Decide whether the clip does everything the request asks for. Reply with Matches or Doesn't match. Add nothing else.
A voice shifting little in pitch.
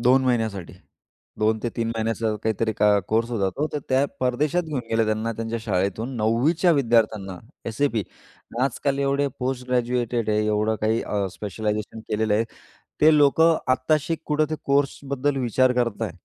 Doesn't match